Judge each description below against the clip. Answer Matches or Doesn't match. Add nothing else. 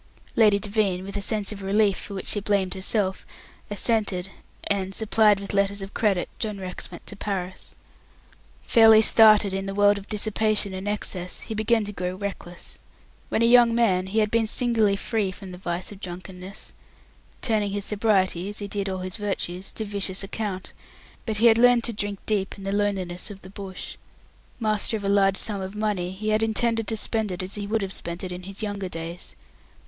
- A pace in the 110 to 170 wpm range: Doesn't match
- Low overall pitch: Doesn't match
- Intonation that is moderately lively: Doesn't match